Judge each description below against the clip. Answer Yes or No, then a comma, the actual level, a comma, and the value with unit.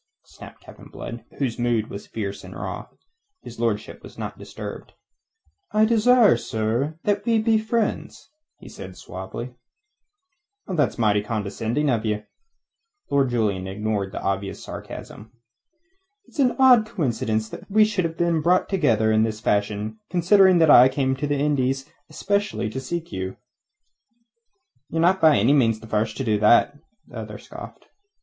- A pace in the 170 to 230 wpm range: No, average, 155 wpm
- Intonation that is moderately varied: No, wide, 8.4 semitones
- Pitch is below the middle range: Yes, low, 130 Hz